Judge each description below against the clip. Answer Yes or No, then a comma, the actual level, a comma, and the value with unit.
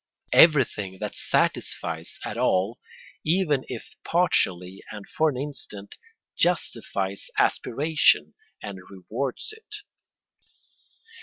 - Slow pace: Yes, slow, 90 wpm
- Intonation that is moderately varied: No, wide, 8.4 semitones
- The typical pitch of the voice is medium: No, low, 120 Hz